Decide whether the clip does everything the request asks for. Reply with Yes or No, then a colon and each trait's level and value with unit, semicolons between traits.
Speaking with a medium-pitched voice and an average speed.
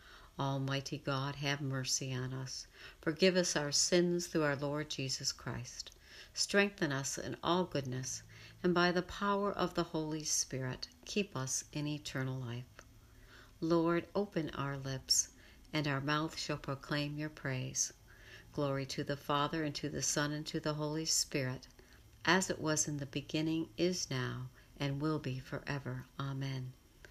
Yes: medium, 145 Hz; average, 155 wpm